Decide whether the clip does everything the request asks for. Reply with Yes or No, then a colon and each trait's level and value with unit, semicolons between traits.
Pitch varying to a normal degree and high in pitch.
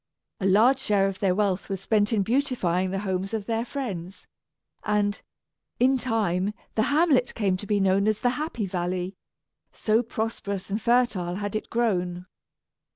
Yes: average, 3.4 semitones; high, 205 Hz